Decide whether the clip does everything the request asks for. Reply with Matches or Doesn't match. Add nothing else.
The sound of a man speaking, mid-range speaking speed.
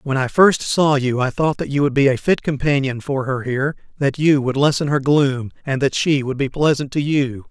Doesn't match